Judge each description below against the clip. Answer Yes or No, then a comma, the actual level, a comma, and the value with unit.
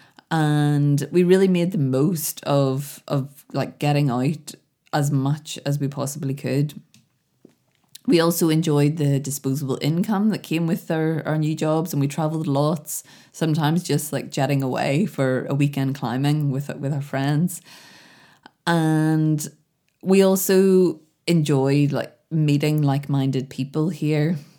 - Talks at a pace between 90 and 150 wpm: Yes, slow, 135 wpm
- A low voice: No, medium, 150 Hz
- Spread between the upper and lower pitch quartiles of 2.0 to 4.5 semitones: Yes, narrow, 2.5 semitones